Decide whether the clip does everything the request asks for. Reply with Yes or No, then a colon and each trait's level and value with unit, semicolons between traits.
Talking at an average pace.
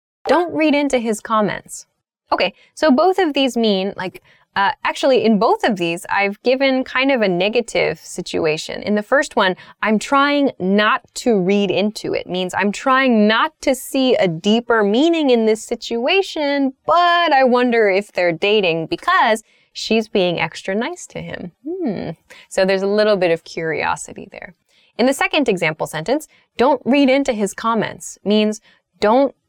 Yes: average, 165 wpm